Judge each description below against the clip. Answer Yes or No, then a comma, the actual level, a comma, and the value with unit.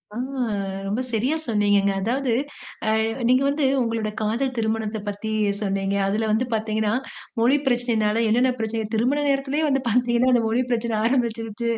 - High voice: Yes, high, 230 Hz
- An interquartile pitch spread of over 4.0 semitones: No, narrow, 2.6 semitones